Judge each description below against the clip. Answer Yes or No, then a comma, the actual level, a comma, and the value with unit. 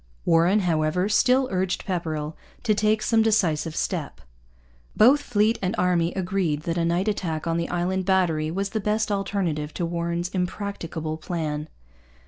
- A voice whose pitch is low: No, medium, 180 Hz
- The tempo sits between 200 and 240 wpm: No, average, 150 wpm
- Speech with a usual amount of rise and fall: Yes, average, 3.5 semitones